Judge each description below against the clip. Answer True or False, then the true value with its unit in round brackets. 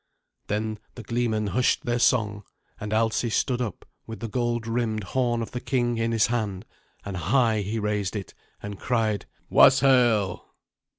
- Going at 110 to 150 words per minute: False (160 wpm)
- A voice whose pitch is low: True (115 Hz)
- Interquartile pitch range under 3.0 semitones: True (2.4 semitones)